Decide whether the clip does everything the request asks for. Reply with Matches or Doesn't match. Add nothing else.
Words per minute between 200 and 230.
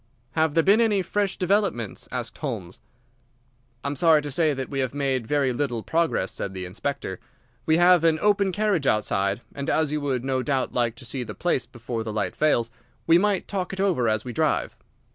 Matches